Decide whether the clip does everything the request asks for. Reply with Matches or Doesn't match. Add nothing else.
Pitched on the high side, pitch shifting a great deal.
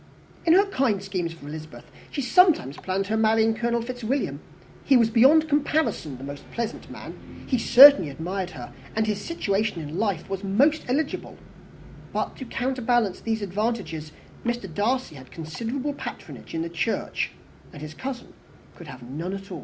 Matches